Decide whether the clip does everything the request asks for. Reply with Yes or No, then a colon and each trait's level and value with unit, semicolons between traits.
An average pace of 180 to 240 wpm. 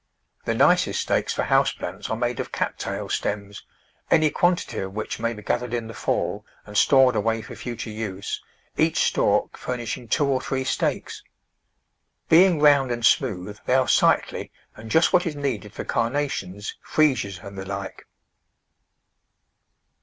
No: average, 160 wpm